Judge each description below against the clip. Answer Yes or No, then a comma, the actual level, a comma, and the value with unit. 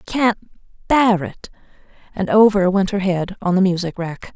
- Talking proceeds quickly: No, average, 180 wpm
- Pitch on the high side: Yes, high, 195 Hz